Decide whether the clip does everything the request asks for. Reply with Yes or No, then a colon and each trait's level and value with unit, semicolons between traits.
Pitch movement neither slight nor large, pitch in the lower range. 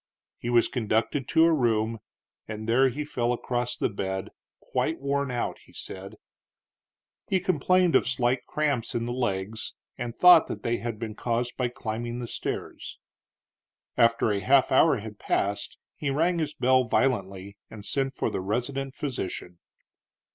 Yes: average, 3.9 semitones; low, 120 Hz